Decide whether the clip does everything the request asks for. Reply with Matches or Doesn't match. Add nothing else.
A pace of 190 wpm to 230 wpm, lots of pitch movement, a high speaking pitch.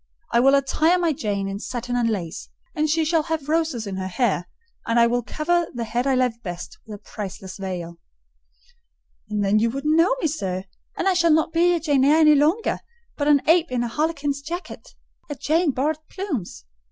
Matches